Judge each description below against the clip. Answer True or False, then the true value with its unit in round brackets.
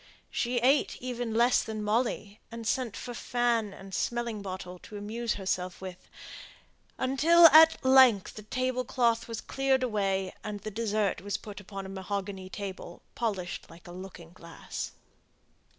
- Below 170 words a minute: True (150 wpm)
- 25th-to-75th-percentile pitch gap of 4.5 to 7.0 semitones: False (3.9 semitones)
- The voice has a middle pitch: False (215 Hz)